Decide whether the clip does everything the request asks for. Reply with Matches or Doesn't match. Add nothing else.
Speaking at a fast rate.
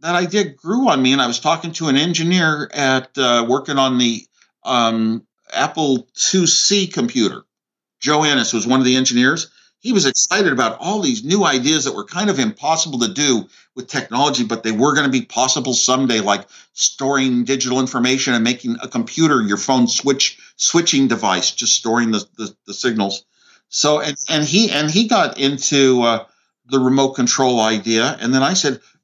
Doesn't match